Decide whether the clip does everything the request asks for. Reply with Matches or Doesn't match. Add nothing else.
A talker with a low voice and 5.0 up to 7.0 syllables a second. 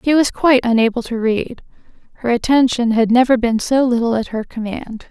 Doesn't match